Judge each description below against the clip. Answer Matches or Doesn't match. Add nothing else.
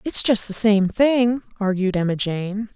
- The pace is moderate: Matches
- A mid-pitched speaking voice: Doesn't match